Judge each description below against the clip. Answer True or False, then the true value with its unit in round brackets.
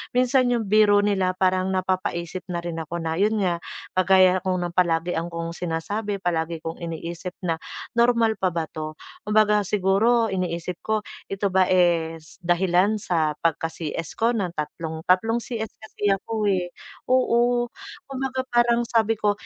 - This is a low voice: False (185 Hz)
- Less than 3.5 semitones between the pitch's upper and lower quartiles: False (4.2 semitones)